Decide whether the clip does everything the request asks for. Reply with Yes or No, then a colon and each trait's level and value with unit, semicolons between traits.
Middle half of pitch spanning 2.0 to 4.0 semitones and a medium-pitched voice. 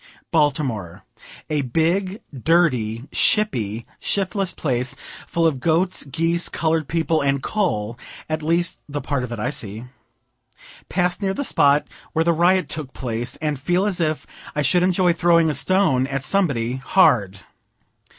No: average, 5.2 semitones; medium, 155 Hz